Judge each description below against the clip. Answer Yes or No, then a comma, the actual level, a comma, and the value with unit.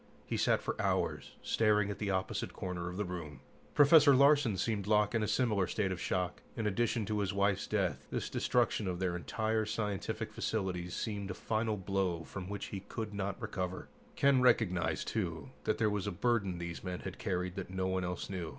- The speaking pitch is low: Yes, low, 100 Hz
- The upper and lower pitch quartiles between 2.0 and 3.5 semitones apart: Yes, average, 2.9 semitones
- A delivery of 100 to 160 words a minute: No, average, 200 wpm